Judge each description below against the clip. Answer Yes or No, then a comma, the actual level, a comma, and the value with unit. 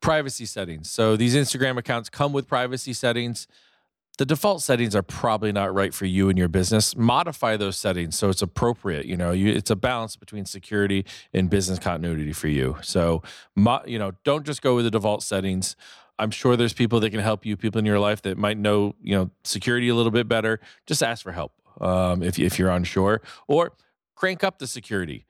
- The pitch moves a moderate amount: Yes, average, 4.0 semitones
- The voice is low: Yes, low, 105 Hz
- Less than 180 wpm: No, fast, 205 wpm